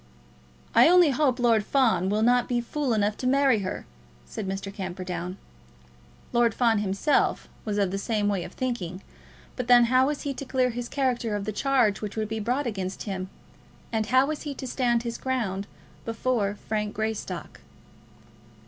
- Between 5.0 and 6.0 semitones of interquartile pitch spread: No, average, 4.0 semitones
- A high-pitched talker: Yes, high, 230 Hz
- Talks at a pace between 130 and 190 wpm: Yes, average, 175 wpm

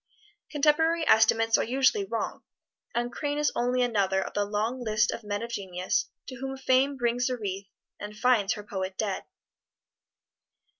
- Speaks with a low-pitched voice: No, high, 235 Hz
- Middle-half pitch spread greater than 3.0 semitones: Yes, average, 4.1 semitones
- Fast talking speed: No, average, 160 wpm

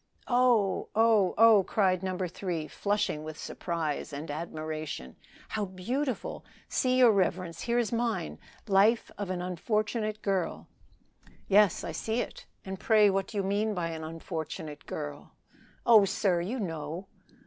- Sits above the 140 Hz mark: Yes, high, 190 Hz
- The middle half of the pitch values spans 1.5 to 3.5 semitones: No, average, 4.6 semitones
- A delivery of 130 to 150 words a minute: Yes, average, 145 wpm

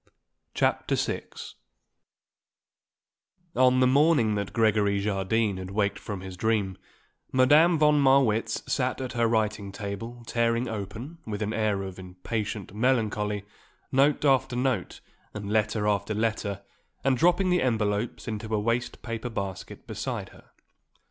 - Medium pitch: No, low, 110 Hz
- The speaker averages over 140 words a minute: No, slow, 135 wpm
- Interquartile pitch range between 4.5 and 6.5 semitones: No, average, 3.8 semitones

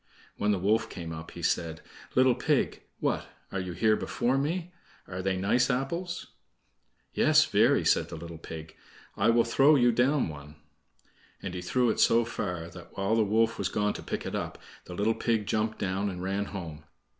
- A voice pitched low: Yes, low, 105 Hz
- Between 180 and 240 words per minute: Yes, average, 190 wpm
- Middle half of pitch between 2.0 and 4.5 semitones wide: No, average, 5.0 semitones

